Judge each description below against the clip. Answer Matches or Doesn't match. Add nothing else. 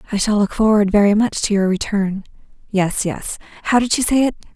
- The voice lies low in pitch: Doesn't match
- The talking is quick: Matches